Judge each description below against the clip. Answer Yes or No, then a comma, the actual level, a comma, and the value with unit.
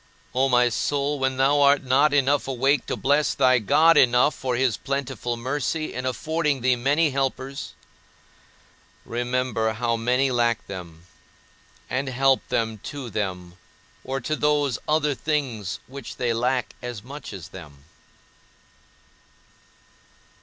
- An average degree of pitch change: Yes, average, 3.0 semitones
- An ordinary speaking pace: No, slow, 130 wpm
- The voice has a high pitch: No, low, 130 Hz